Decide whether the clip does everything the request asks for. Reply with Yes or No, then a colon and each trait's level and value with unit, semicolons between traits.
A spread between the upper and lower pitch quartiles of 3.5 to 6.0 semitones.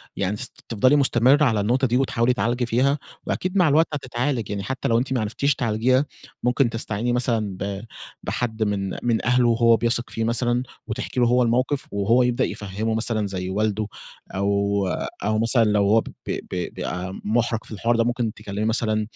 No: average, 3.0 semitones